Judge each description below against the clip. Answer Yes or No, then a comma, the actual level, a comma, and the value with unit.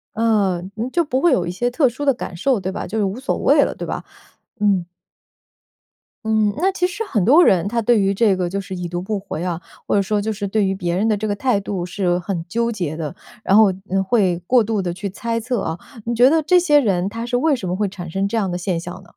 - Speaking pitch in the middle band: No, high, 205 Hz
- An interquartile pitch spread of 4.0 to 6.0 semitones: Yes, average, 4.5 semitones